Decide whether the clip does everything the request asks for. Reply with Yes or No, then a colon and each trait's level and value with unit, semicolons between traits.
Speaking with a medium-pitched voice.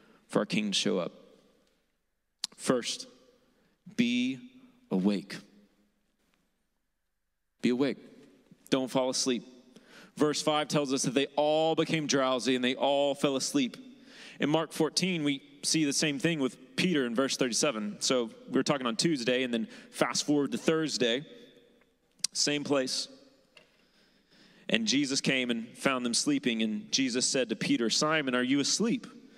Yes: medium, 145 Hz